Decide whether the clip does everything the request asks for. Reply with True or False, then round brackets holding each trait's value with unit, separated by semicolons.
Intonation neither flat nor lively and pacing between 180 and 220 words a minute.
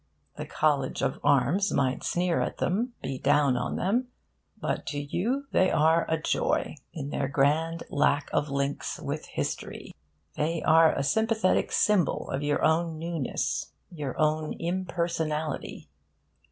False (3.3 semitones; 140 wpm)